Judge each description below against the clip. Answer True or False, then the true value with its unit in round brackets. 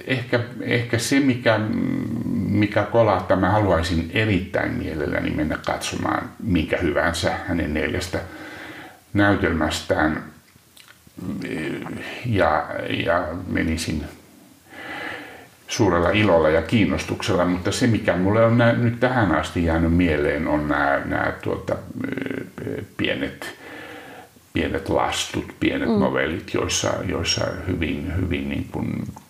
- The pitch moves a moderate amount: False (5.7 semitones)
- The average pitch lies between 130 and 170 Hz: False (100 Hz)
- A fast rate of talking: False (100 wpm)